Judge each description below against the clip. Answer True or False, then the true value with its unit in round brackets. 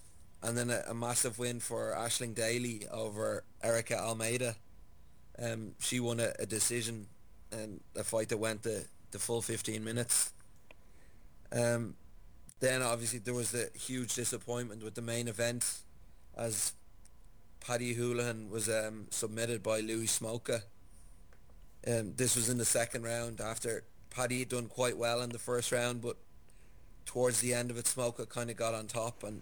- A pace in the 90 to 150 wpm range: False (165 wpm)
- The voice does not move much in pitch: True (1.8 semitones)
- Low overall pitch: True (115 Hz)